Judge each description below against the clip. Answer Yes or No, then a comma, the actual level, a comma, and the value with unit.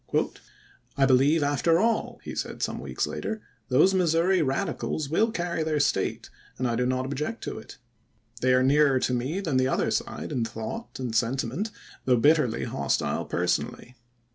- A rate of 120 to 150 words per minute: No, average, 185 wpm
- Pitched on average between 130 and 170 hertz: Yes, medium, 140 Hz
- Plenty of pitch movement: No, average, 4.7 semitones